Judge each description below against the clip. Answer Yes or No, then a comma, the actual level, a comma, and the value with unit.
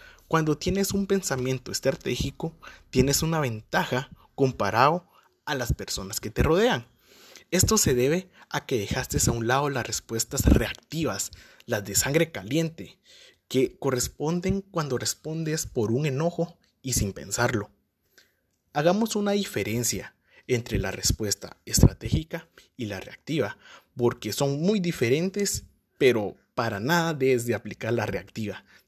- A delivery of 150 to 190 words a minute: No, average, 130 wpm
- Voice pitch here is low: Yes, low, 130 Hz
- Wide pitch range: Yes, wide, 6.1 semitones